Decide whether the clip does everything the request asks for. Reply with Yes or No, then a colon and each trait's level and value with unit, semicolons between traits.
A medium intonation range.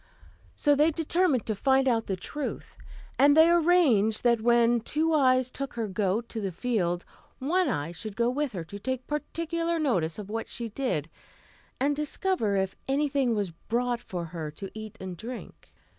No: wide, 6.3 semitones